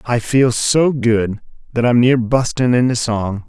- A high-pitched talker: No, low, 120 Hz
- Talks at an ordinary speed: Yes, average, 170 wpm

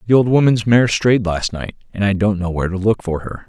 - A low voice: Yes, low, 105 Hz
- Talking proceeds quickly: Yes, fast, 275 wpm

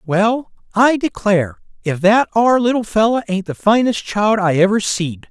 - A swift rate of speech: No, average, 170 wpm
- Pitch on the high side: Yes, high, 205 Hz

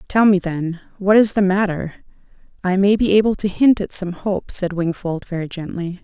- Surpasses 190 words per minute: Yes, average, 200 wpm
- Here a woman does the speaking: Yes, female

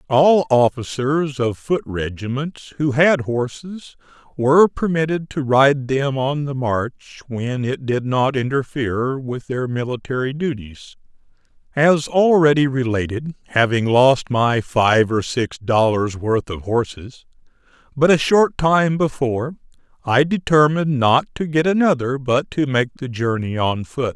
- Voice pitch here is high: No, low, 135 Hz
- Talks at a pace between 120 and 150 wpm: Yes, average, 140 wpm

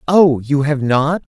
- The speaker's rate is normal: Yes, average, 180 wpm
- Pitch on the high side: No, medium, 145 Hz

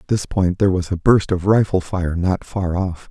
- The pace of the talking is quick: Yes, fast, 250 wpm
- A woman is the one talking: No, male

